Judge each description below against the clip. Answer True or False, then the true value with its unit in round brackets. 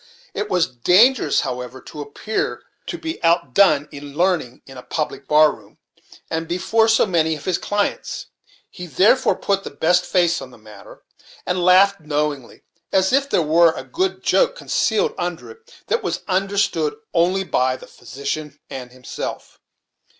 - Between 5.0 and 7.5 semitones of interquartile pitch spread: True (5.6 semitones)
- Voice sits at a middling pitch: True (170 Hz)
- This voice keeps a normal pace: True (165 wpm)